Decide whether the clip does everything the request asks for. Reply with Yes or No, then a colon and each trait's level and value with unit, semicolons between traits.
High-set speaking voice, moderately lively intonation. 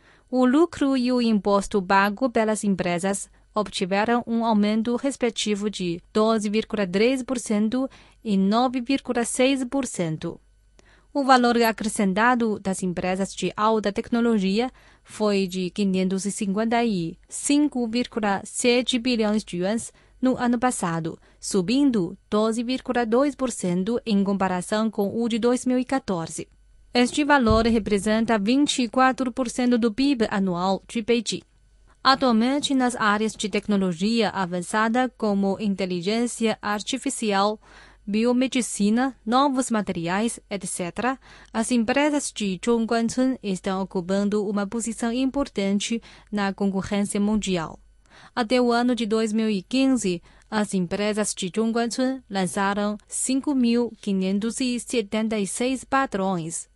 Yes: high, 220 Hz; average, 3.8 semitones